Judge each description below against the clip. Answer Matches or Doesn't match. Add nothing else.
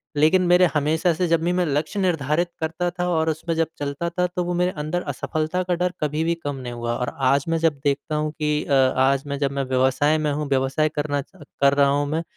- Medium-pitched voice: Matches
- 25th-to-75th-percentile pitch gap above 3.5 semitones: Doesn't match